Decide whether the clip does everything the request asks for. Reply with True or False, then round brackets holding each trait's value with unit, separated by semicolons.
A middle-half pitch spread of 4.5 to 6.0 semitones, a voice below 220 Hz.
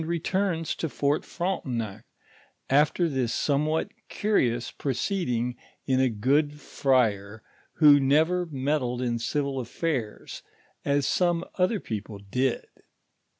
True (4.9 semitones; 140 Hz)